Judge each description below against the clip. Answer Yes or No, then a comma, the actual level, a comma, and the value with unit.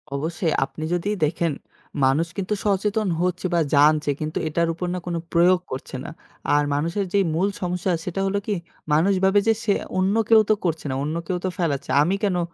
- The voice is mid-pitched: Yes, medium, 175 Hz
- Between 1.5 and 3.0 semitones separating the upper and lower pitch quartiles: No, average, 3.7 semitones